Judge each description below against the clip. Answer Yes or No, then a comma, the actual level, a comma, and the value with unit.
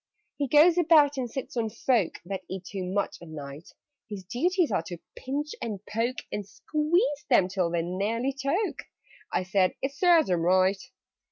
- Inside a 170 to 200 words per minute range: Yes, average, 175 wpm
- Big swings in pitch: Yes, wide, 7.8 semitones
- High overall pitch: Yes, high, 230 Hz